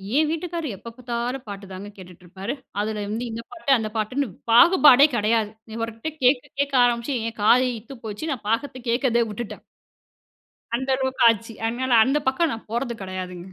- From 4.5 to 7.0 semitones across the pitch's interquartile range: No, average, 3.7 semitones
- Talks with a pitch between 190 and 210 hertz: No, high, 235 Hz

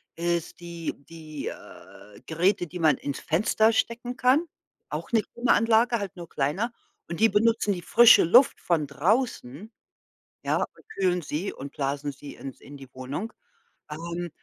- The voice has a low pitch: No, medium, 175 Hz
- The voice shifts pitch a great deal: Yes, wide, 7.0 semitones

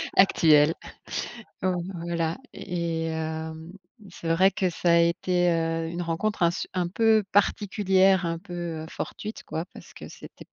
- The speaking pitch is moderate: Yes, medium, 170 Hz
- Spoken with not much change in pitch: Yes, narrow, 2.3 semitones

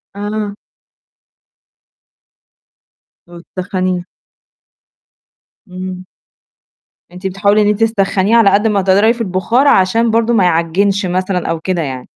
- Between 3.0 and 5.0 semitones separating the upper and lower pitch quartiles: No, narrow, 2.5 semitones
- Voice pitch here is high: Yes, high, 195 Hz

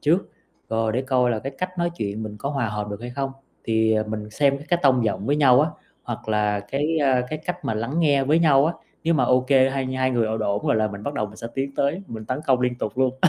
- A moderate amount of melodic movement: Yes, average, 4.4 semitones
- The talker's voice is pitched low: Yes, low, 130 Hz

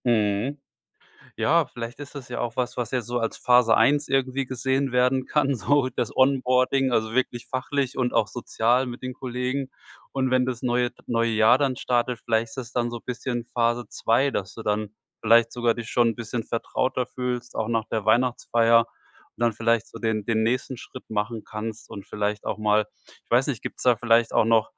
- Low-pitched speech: Yes, low, 120 Hz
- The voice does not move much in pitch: Yes, narrow, 2.1 semitones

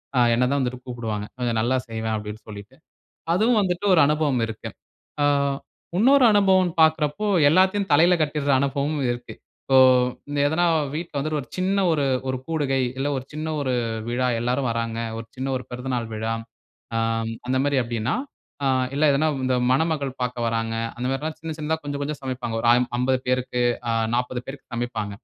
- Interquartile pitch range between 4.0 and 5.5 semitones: Yes, average, 4.3 semitones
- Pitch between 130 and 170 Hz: Yes, low, 135 Hz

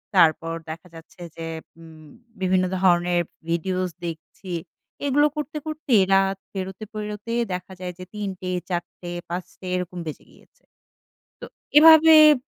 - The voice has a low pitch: No, medium, 185 Hz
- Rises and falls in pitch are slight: No, average, 3.3 semitones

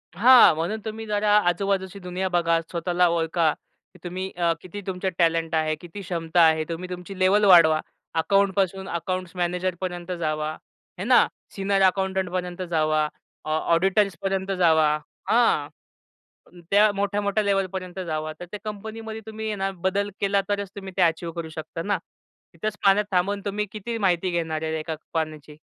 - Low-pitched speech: No, medium, 185 Hz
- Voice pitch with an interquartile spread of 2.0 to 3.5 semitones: Yes, average, 3.1 semitones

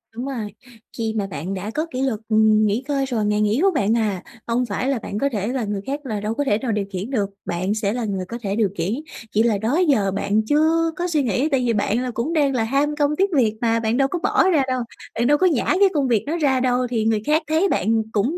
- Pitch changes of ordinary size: Yes, average, 4.9 semitones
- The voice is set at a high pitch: Yes, high, 235 Hz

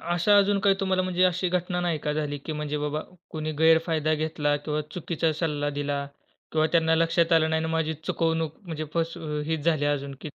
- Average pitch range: No, narrow, 1.9 semitones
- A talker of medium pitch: Yes, medium, 160 Hz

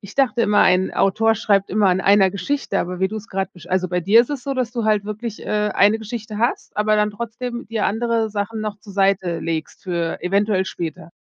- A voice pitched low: No, high, 205 Hz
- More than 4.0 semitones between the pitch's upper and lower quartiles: No, average, 2.9 semitones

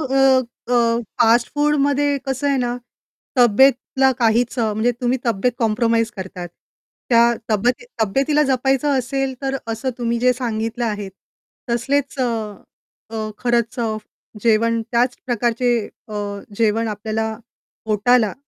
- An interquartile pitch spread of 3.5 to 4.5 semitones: No, average, 2.8 semitones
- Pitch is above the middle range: Yes, high, 240 Hz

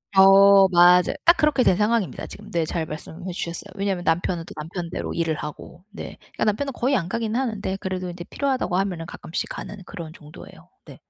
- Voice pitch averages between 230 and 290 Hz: No, medium, 185 Hz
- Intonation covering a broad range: No, average, 3.8 semitones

